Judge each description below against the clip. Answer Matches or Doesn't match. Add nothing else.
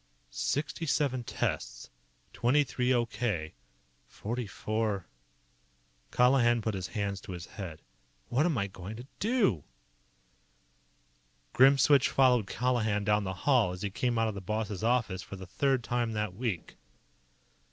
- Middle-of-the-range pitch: Doesn't match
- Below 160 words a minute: Matches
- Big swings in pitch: Doesn't match